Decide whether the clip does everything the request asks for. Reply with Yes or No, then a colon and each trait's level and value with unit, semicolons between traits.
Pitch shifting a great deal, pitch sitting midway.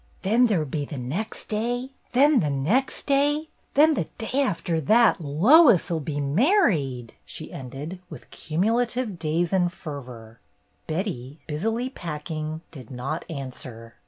Yes: wide, 8.8 semitones; medium, 170 Hz